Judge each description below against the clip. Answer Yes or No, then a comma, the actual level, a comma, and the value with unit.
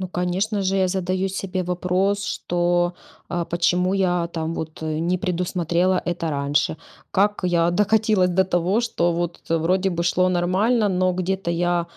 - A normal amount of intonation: No, narrow, 1.7 semitones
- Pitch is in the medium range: Yes, medium, 180 Hz